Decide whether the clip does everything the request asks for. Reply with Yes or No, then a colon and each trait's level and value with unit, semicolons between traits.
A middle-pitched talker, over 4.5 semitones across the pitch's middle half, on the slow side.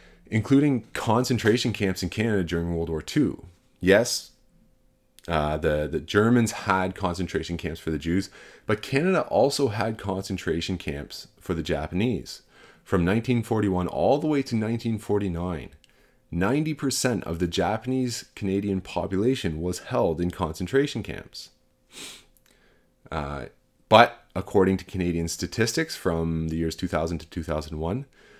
No: very low, 95 Hz; average, 5.3 semitones; slow, 125 wpm